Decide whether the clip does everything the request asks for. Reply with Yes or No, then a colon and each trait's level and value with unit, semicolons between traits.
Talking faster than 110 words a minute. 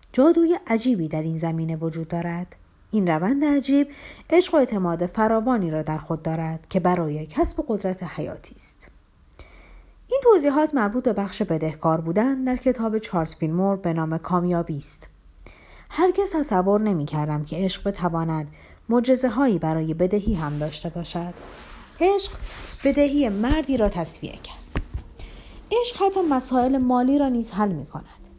Yes: average, 140 wpm